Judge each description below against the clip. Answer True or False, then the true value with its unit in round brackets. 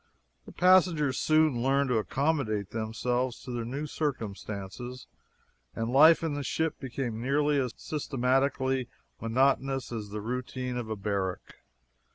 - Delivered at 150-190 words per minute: False (135 wpm)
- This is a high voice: False (130 Hz)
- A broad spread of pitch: False (3.7 semitones)